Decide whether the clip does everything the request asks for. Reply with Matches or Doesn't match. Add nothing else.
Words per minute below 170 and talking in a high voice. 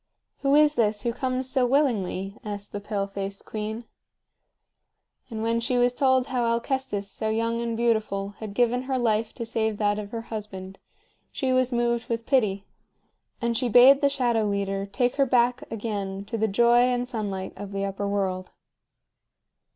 Doesn't match